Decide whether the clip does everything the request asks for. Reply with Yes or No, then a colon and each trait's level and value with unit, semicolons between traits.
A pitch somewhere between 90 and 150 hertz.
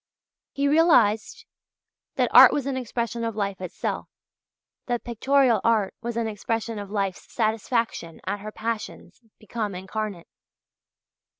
No: high, 225 Hz